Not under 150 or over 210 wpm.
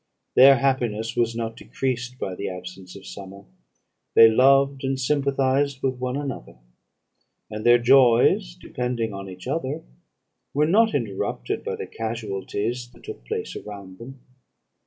No: average, 140 wpm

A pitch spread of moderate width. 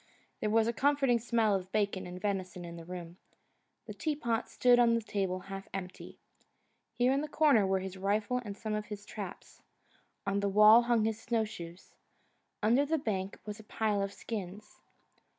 Yes: average, 3.3 semitones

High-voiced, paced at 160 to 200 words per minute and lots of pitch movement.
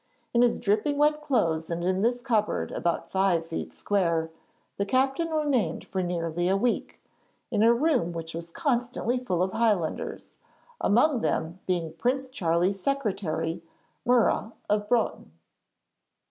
No: high, 205 Hz; average, 140 wpm; wide, 6.4 semitones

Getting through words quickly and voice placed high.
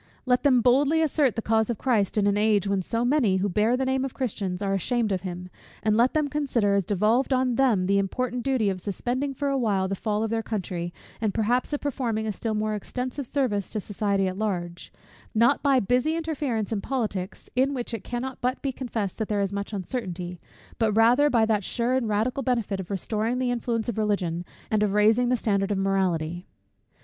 Yes: fast, 215 wpm; high, 220 Hz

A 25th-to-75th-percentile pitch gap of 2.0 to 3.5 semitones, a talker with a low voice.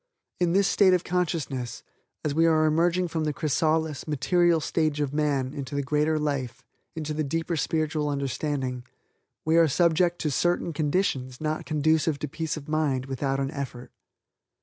No: average, 2.7 semitones; medium, 155 Hz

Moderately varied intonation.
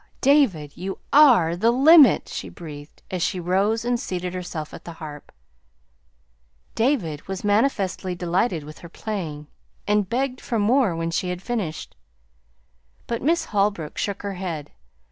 No: wide, 5.8 semitones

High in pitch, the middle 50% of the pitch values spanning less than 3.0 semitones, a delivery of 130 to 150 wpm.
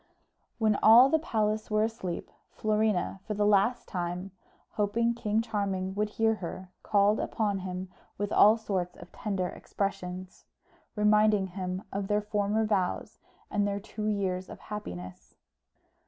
Yes: high, 205 Hz; narrow, 2.4 semitones; average, 140 wpm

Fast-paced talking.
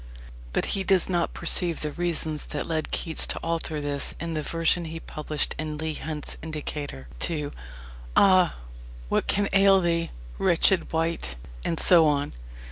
No: average, 155 wpm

